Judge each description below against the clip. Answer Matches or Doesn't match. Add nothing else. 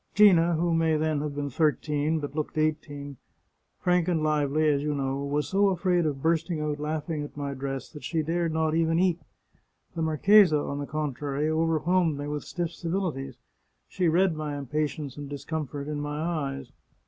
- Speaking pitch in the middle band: Matches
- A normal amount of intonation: Doesn't match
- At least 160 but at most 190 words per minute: Matches